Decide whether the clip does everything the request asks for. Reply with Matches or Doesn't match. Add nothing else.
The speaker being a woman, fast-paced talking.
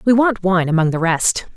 Matches